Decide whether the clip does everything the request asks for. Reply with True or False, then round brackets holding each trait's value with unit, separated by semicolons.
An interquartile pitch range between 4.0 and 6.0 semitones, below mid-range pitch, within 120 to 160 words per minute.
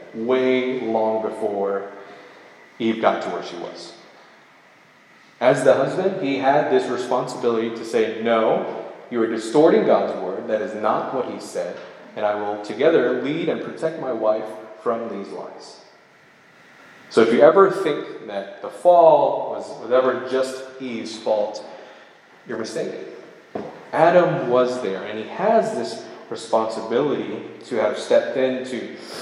False (3.4 semitones; 125 Hz; 145 wpm)